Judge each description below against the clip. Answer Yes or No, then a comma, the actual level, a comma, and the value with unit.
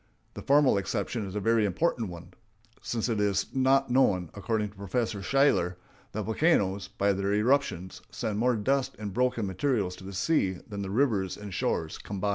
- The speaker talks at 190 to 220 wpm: No, average, 180 wpm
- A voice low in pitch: Yes, low, 105 Hz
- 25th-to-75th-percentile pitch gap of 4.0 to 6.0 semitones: Yes, average, 4.5 semitones